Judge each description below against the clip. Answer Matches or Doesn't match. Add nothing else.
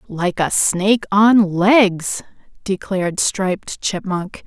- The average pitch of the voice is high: Matches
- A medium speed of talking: Doesn't match